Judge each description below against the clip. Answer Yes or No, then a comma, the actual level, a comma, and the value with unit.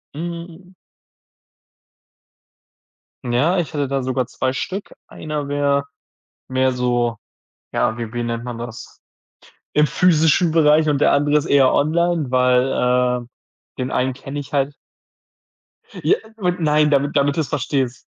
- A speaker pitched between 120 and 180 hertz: Yes, medium, 140 Hz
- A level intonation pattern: No, average, 3.4 semitones